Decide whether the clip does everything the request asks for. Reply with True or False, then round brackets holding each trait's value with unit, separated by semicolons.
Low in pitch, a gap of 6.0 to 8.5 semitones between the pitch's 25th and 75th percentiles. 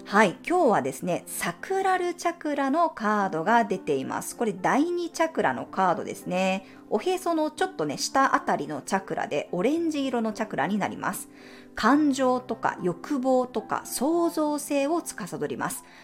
False (275 Hz; 6.6 semitones)